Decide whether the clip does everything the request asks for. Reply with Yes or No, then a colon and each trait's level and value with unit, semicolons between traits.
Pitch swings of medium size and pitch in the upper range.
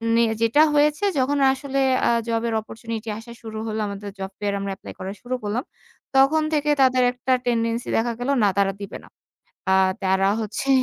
Yes: average, 4.2 semitones; high, 230 Hz